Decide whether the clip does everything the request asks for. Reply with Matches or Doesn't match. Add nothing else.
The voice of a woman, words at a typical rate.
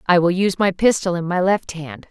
Doesn't match